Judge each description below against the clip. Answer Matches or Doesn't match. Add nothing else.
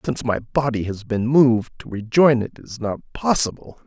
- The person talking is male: Matches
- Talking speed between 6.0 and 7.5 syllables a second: Doesn't match